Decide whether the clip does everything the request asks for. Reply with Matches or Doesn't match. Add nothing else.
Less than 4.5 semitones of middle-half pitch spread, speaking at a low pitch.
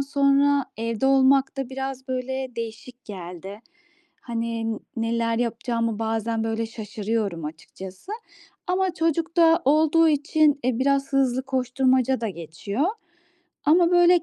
Doesn't match